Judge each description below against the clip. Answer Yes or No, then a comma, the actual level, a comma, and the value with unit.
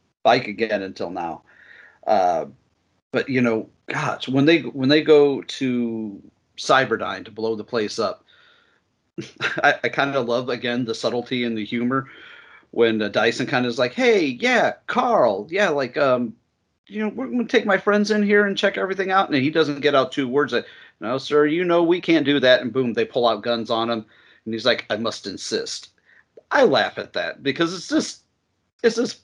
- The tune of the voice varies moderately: No, wide, 8.0 semitones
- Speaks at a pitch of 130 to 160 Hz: Yes, medium, 140 Hz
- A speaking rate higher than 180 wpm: Yes, average, 200 wpm